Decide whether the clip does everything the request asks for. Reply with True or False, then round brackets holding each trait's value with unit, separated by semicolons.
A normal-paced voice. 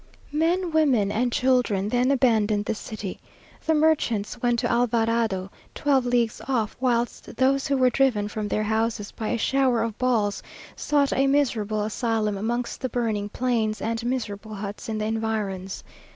True (160 wpm)